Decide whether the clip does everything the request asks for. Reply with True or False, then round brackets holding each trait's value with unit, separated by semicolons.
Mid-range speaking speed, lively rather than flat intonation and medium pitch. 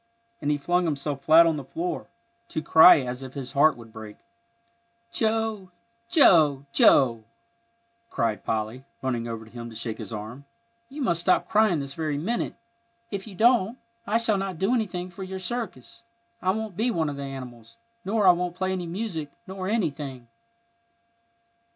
True (170 wpm; 6.8 semitones; 165 Hz)